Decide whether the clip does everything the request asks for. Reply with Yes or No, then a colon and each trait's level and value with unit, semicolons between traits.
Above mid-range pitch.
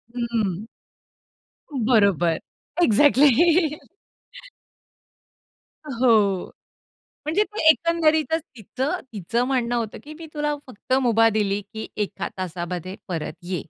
Yes: high, 235 Hz